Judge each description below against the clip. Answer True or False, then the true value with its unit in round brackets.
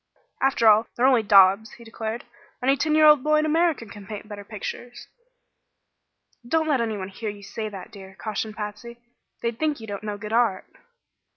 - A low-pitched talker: False (225 Hz)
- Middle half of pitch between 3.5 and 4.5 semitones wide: True (3.8 semitones)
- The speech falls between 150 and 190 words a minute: True (185 wpm)